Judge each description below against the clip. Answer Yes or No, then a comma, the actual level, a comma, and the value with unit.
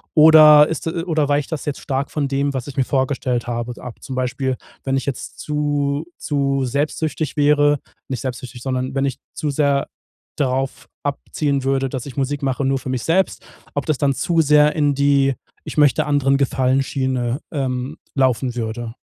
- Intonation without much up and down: Yes, narrow, 2.0 semitones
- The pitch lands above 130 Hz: Yes, medium, 140 Hz